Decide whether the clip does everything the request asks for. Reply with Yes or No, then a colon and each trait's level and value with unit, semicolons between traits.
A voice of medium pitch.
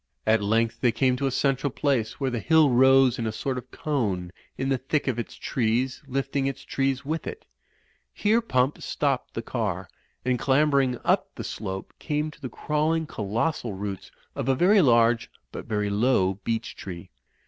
No: low, 130 Hz